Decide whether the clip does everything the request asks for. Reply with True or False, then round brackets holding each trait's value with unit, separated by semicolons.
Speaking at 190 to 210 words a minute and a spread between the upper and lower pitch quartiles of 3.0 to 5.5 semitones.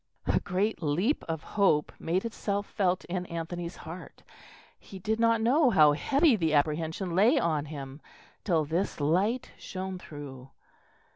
False (145 wpm; 5.1 semitones)